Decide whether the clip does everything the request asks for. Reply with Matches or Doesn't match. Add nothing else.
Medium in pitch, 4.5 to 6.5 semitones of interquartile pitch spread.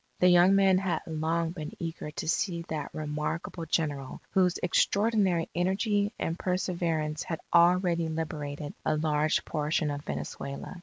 Doesn't match